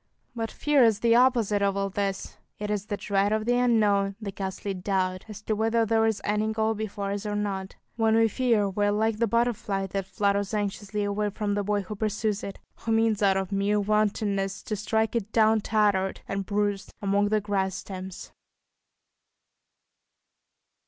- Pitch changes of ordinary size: No, narrow, 1.8 semitones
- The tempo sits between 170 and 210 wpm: Yes, average, 185 wpm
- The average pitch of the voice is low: No, high, 205 Hz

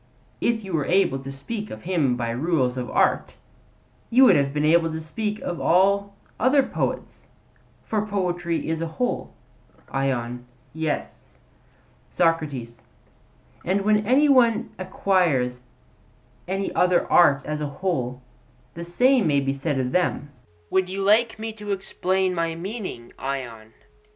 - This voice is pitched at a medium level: Yes, medium, 170 Hz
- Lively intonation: Yes, wide, 6.5 semitones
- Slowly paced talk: No, average, 145 wpm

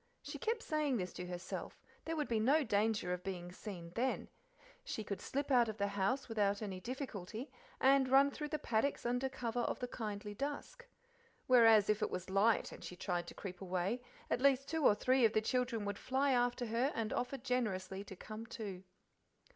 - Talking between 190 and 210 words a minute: Yes, average, 195 wpm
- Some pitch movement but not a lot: Yes, average, 4.7 semitones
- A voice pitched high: Yes, high, 225 Hz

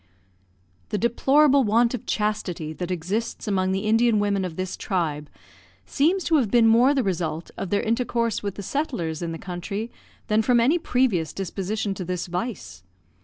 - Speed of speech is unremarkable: Yes, average, 170 wpm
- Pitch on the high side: Yes, high, 205 Hz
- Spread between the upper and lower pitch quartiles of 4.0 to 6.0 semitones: Yes, average, 4.8 semitones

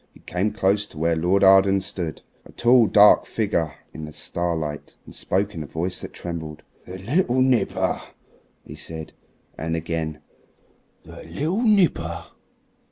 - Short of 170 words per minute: Yes, average, 150 wpm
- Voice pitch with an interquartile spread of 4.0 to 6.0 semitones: Yes, average, 4.3 semitones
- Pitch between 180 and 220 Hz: No, very low, 90 Hz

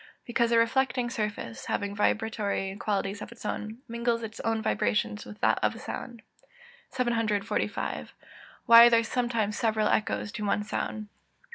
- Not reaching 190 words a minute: Yes, average, 155 wpm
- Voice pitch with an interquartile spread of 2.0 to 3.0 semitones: Yes, narrow, 2.4 semitones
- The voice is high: Yes, high, 220 Hz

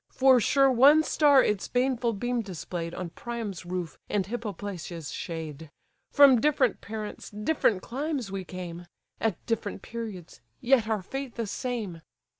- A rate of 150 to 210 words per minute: No, average, 140 wpm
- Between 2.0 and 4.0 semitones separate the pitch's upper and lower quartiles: No, wide, 5.5 semitones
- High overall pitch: Yes, high, 220 Hz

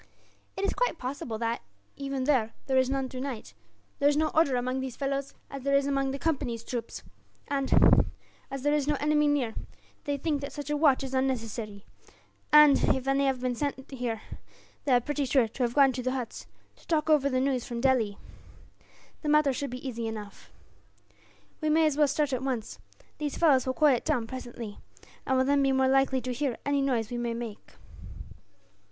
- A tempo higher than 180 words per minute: Yes, average, 200 wpm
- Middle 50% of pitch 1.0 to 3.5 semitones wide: Yes, narrow, 2.5 semitones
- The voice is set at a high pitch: Yes, very high, 265 Hz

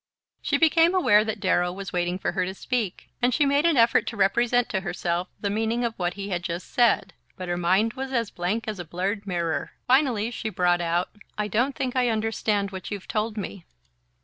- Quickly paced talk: Yes, fast, 215 wpm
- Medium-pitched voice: No, high, 210 Hz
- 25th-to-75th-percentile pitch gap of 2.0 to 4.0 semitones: No, average, 4.5 semitones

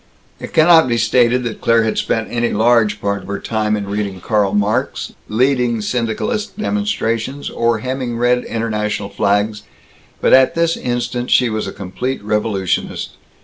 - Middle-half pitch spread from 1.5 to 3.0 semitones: Yes, average, 2.7 semitones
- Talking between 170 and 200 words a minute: No, average, 155 wpm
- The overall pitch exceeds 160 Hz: No, low, 115 Hz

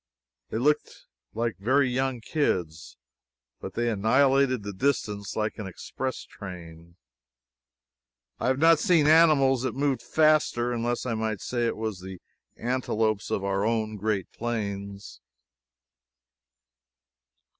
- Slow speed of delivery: Yes, slow, 120 wpm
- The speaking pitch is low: Yes, low, 115 Hz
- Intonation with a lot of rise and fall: No, average, 4.7 semitones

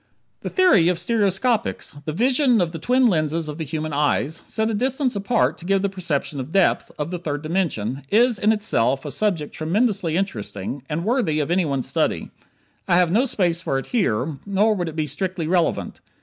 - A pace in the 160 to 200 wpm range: Yes, average, 195 wpm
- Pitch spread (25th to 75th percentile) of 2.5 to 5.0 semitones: No, wide, 5.5 semitones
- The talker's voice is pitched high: No, medium, 175 Hz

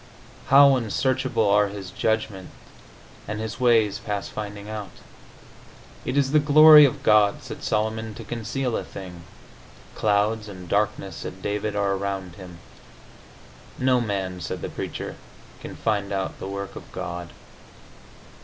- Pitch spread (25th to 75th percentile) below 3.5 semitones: Yes, average, 2.8 semitones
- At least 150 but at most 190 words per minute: No, average, 140 wpm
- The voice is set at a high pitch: No, low, 105 Hz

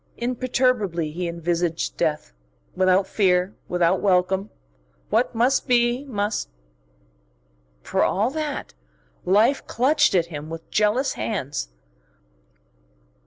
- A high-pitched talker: Yes, high, 195 Hz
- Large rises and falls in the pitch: Yes, wide, 5.7 semitones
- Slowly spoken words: Yes, slow, 100 wpm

